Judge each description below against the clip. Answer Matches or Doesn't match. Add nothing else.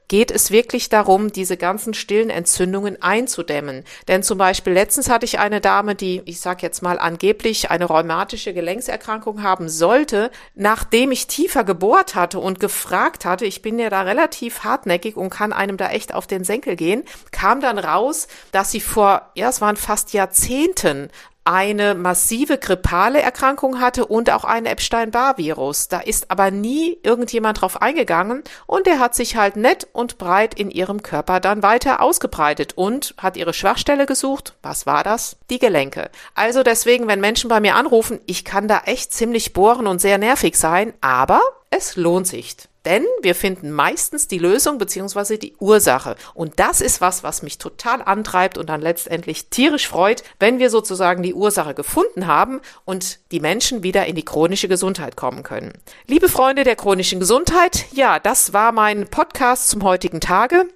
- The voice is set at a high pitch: Matches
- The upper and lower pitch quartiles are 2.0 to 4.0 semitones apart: Doesn't match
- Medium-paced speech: Matches